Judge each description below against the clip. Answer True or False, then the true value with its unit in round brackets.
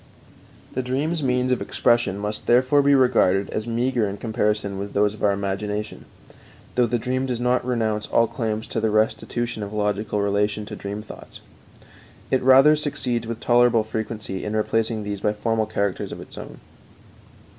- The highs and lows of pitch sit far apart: False (3.0 semitones)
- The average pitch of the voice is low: True (110 Hz)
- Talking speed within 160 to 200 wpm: True (175 wpm)